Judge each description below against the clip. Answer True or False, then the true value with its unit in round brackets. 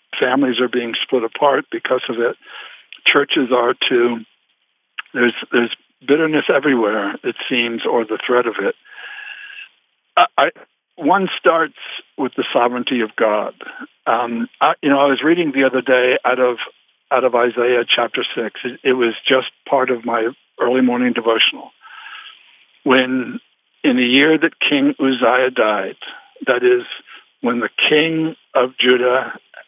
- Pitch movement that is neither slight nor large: True (3.6 semitones)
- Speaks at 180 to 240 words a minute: False (150 wpm)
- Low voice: True (130 Hz)